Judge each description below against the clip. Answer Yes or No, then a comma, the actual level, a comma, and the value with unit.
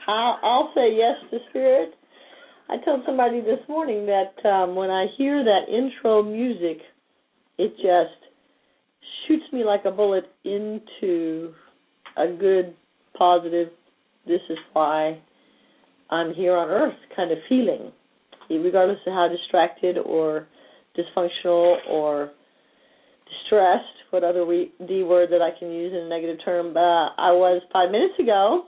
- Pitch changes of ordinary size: Yes, average, 4.0 semitones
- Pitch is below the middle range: No, medium, 180 Hz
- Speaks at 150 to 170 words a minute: No, average, 140 wpm